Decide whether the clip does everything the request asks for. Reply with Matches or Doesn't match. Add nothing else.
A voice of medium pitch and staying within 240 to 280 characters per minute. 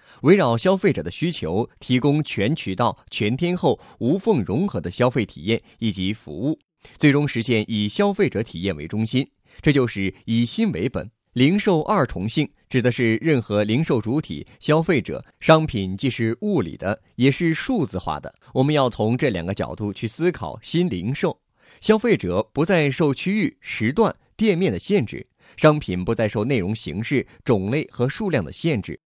Doesn't match